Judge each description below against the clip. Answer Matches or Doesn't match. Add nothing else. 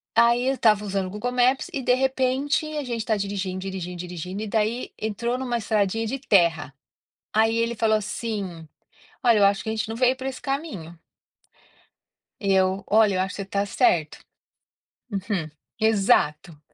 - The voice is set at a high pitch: Matches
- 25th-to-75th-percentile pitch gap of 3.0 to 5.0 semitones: Matches